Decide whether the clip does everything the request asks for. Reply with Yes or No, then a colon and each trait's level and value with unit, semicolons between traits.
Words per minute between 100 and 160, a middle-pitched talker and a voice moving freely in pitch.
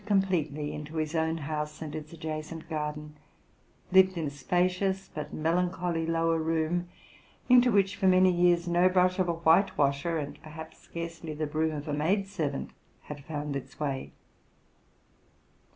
No: average, 155 wpm; medium, 165 Hz; average, 3.0 semitones